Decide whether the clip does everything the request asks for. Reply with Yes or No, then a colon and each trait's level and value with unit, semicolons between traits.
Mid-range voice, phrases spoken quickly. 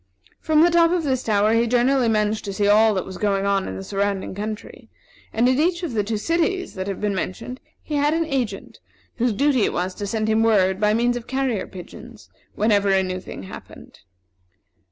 No: high, 220 Hz; fast, 215 wpm